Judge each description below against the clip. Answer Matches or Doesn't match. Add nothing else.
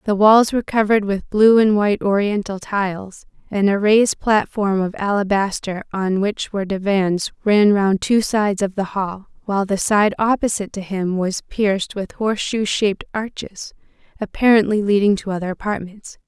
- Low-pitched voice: Doesn't match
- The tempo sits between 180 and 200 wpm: Doesn't match